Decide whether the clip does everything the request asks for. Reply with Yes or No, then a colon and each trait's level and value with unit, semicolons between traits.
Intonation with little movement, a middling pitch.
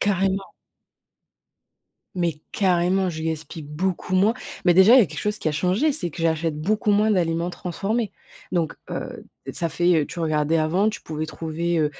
No: average, 3.4 semitones; medium, 175 Hz